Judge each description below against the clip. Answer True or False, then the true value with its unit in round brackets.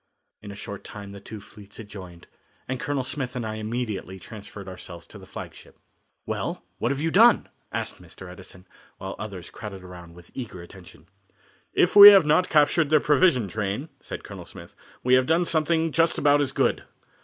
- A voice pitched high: False (110 Hz)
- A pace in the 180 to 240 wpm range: True (190 wpm)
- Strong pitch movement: True (7.3 semitones)